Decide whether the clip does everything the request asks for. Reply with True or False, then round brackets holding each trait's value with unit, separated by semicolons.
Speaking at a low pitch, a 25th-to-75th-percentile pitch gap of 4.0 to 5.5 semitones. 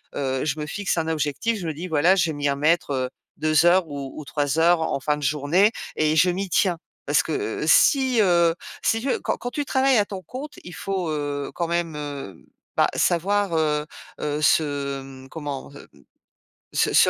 False (160 Hz; 4.3 semitones)